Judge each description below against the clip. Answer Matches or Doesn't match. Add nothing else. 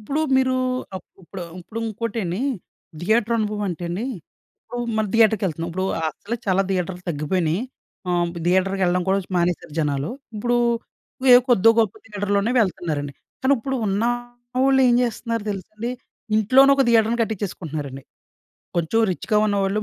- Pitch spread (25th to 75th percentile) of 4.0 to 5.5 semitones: Matches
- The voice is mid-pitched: Doesn't match